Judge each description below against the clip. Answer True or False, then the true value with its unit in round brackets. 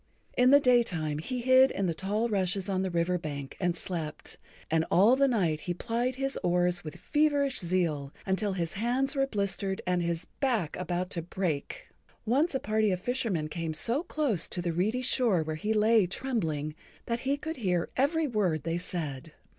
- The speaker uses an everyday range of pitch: False (6.6 semitones)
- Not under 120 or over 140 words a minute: False (185 wpm)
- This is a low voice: False (190 Hz)